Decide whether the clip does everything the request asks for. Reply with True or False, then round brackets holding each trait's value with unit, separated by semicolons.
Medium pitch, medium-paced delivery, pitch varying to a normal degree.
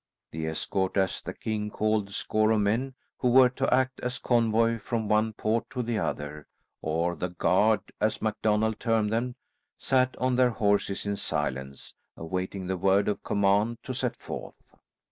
False (110 Hz; 170 wpm; 3.2 semitones)